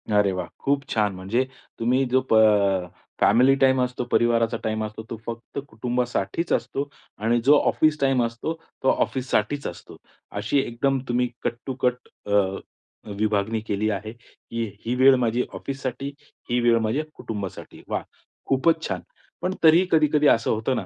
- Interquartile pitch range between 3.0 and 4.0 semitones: Yes, average, 3.6 semitones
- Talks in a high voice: No, low, 120 Hz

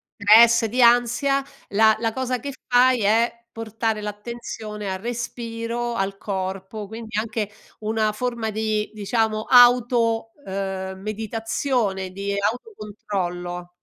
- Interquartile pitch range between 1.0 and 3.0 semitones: Yes, narrow, 2.6 semitones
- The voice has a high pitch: Yes, high, 220 Hz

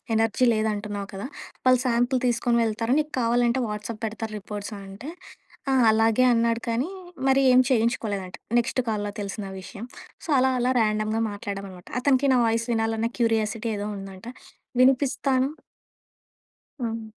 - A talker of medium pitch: No, high, 225 Hz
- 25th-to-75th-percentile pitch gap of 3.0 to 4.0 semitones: No, narrow, 2.6 semitones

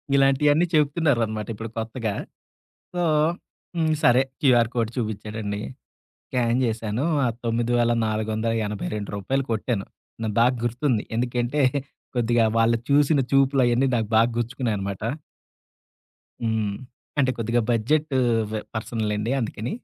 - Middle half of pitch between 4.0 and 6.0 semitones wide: No, average, 3.0 semitones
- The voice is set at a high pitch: No, low, 115 Hz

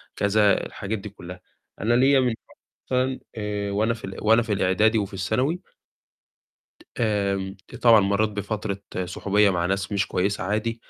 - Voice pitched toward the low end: Yes, low, 105 Hz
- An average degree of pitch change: No, narrow, 2.3 semitones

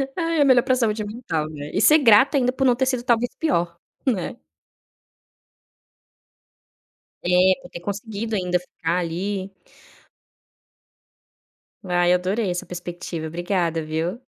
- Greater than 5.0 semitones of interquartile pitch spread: Yes, wide, 5.6 semitones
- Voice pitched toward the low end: No, high, 190 Hz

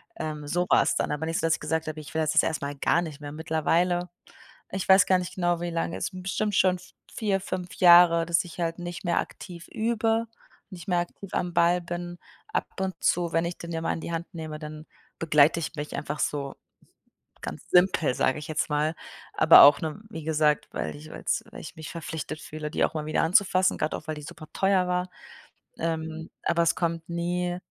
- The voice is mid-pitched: Yes, medium, 170 Hz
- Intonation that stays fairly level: Yes, narrow, 2.3 semitones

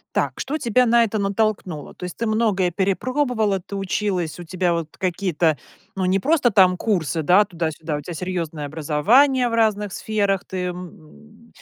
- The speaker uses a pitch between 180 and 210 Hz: Yes, high, 190 Hz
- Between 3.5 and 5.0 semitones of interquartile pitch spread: Yes, average, 4.2 semitones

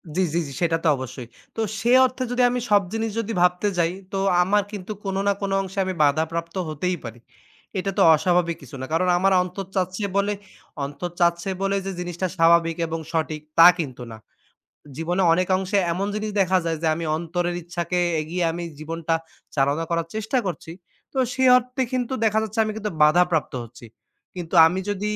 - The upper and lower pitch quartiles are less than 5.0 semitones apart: Yes, average, 3.3 semitones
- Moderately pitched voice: Yes, medium, 180 Hz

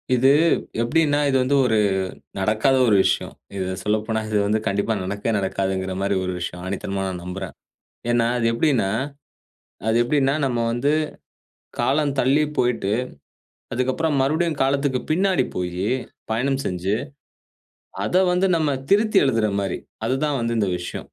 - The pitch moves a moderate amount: No, wide, 6.1 semitones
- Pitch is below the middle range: Yes, low, 115 Hz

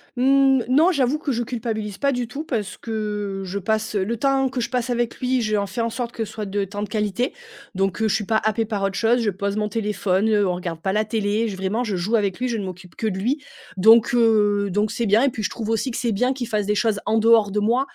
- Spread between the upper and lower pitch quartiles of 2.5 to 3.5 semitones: Yes, average, 2.9 semitones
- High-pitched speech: Yes, high, 220 Hz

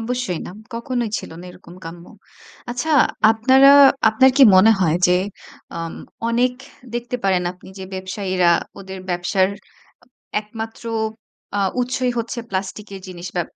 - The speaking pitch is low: No, high, 205 Hz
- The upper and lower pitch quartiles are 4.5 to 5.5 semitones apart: Yes, average, 4.8 semitones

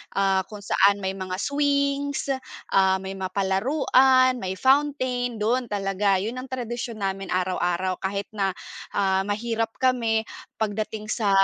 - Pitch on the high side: Yes, high, 210 Hz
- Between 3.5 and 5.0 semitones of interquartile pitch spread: Yes, average, 4.7 semitones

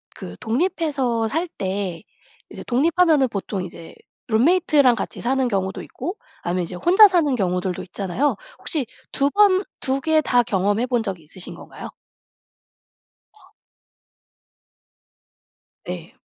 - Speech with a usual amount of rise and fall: No, wide, 8.4 semitones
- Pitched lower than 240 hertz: No, high, 245 Hz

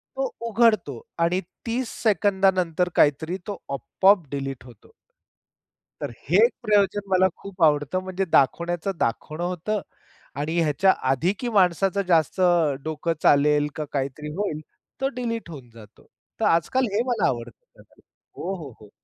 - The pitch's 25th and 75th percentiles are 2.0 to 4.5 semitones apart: No, average, 5.2 semitones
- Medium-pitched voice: Yes, medium, 175 Hz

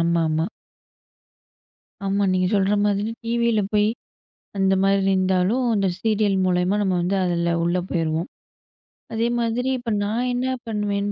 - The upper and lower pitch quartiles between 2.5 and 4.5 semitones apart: Yes, average, 3.5 semitones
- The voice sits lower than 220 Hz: Yes, high, 200 Hz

